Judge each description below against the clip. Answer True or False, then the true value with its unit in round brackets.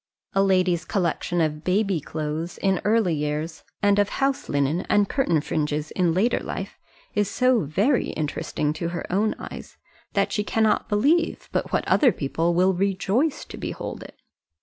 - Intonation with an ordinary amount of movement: True (4.7 semitones)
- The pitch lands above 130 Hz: True (185 Hz)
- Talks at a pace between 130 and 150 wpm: False (165 wpm)